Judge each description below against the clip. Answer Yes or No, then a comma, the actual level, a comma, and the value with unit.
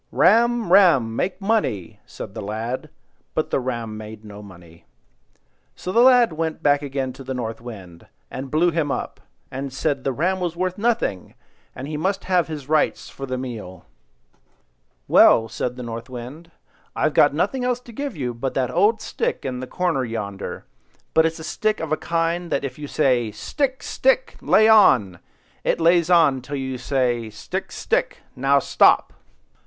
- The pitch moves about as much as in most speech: No, wide, 6.6 semitones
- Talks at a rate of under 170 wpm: No, average, 175 wpm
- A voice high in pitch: No, medium, 140 Hz